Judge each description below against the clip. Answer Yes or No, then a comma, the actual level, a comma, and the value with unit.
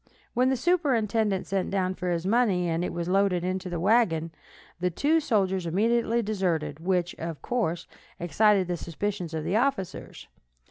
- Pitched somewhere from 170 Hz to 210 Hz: Yes, high, 190 Hz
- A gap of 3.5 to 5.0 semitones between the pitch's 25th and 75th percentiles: Yes, average, 4.2 semitones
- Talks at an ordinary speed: Yes, average, 165 wpm